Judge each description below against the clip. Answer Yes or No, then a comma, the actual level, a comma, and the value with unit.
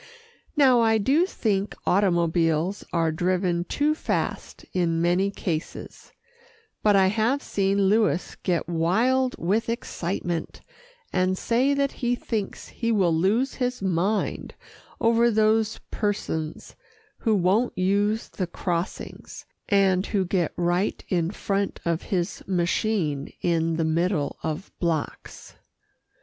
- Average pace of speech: No, slow, 120 wpm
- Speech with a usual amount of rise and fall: Yes, average, 4.3 semitones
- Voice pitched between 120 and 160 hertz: No, high, 190 Hz